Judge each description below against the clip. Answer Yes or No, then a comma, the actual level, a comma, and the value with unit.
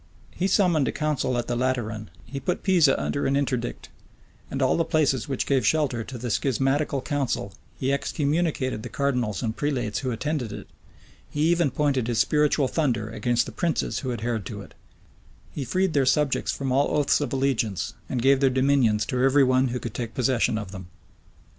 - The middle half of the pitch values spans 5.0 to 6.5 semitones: No, average, 3.4 semitones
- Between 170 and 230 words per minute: Yes, average, 190 wpm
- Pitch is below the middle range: Yes, low, 130 Hz